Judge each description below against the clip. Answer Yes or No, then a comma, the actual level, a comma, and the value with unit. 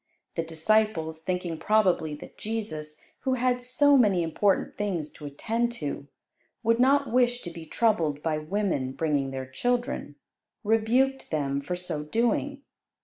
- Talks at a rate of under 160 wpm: Yes, average, 145 wpm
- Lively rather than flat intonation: Yes, wide, 7.4 semitones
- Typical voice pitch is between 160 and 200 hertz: Yes, high, 190 Hz